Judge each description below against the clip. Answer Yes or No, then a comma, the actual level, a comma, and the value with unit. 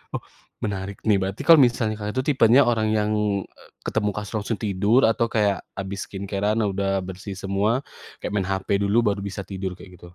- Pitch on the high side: No, low, 100 Hz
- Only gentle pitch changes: Yes, narrow, 2.0 semitones